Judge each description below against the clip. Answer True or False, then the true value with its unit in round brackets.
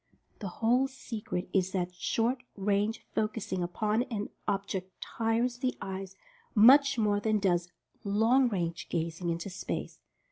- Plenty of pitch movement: False (3.6 semitones)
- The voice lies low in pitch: False (205 Hz)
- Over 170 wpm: False (135 wpm)